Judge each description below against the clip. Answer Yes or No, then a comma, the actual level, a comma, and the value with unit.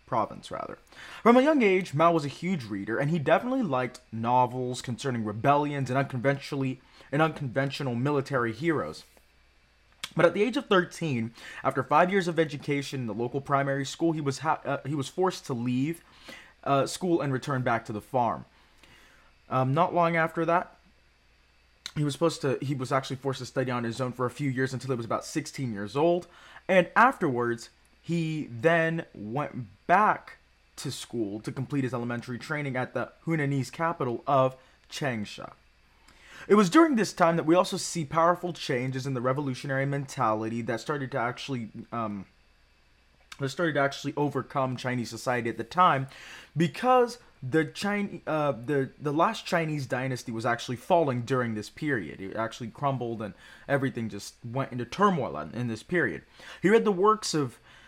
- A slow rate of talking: No, average, 175 wpm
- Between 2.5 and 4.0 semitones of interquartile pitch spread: No, average, 5.2 semitones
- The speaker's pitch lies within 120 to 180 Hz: Yes, low, 135 Hz